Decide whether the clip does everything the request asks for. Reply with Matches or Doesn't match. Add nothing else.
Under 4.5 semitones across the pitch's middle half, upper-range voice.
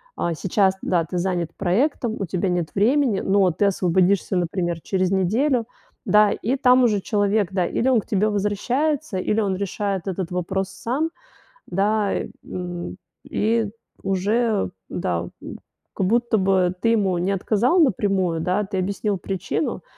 Matches